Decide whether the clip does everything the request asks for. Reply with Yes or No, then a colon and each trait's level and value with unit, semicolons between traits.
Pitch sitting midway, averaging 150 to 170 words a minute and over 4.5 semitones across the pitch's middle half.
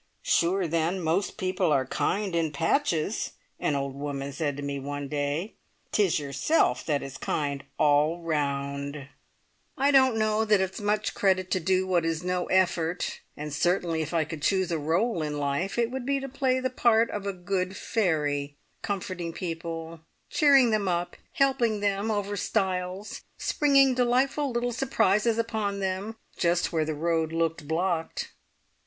Yes: medium, 180 Hz; average, 160 wpm; average, 5.3 semitones